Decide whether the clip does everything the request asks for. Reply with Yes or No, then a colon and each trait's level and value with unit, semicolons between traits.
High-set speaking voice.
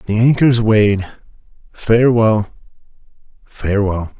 No: low, 110 Hz